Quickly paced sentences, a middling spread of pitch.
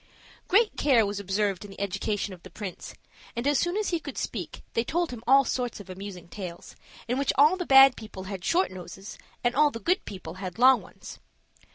No: fast, 215 wpm; wide, 6.3 semitones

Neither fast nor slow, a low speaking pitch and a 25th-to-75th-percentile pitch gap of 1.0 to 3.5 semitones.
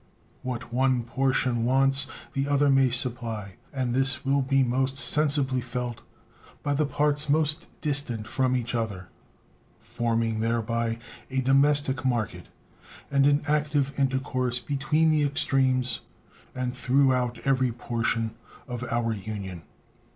No: slow, 125 wpm; low, 130 Hz; average, 2.8 semitones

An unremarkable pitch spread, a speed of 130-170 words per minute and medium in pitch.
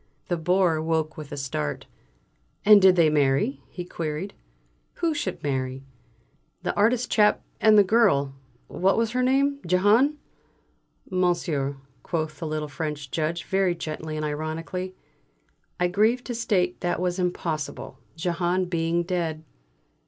Yes: average, 4.1 semitones; average, 140 wpm; medium, 175 Hz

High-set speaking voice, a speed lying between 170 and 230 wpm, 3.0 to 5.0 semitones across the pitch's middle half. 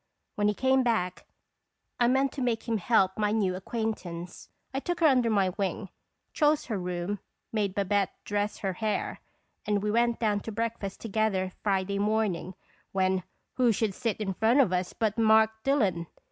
Yes: high, 210 Hz; average, 175 wpm; average, 3.3 semitones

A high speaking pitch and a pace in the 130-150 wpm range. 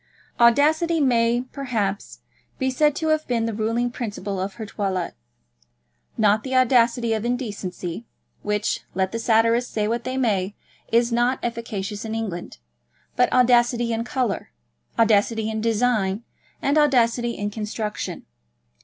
Yes: high, 230 Hz; slow, 135 wpm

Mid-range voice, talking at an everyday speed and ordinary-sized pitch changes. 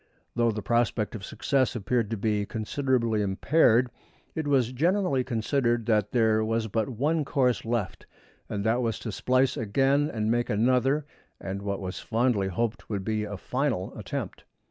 No: low, 115 Hz; average, 165 wpm; average, 3.3 semitones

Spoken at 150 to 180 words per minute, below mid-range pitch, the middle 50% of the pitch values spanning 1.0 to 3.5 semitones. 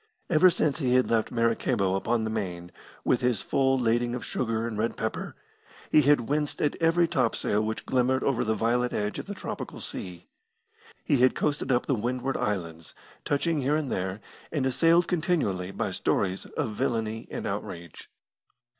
No: average, 170 wpm; low, 120 Hz; average, 4.5 semitones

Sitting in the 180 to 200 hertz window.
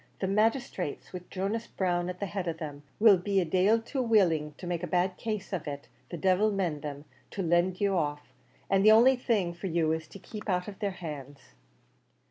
Yes: medium, 185 Hz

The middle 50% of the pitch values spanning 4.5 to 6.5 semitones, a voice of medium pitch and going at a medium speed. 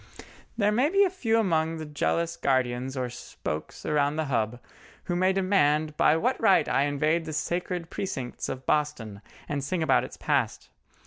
Yes: average, 5.1 semitones; medium, 155 Hz; average, 175 wpm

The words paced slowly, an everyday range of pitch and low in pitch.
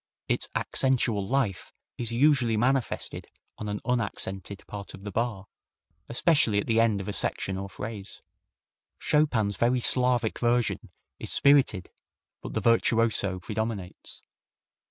Yes: slow, 130 wpm; average, 3.4 semitones; low, 115 Hz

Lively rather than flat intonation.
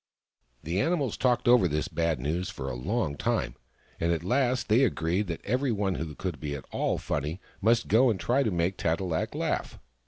Yes: wide, 6.7 semitones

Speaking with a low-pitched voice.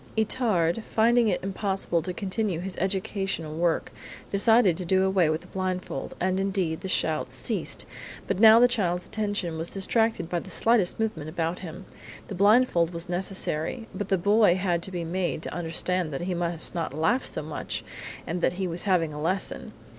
No: medium, 185 Hz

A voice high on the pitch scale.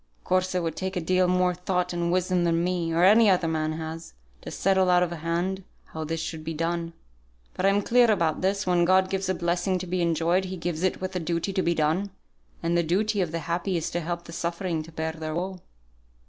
No: medium, 175 Hz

